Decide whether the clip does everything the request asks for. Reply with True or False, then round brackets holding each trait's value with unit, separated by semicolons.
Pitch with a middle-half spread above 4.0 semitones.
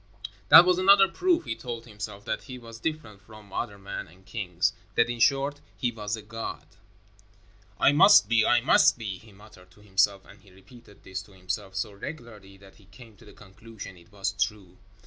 False (3.6 semitones)